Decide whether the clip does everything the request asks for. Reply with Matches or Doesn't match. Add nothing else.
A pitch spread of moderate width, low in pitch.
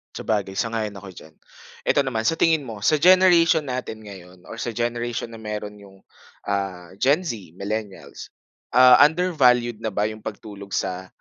Matches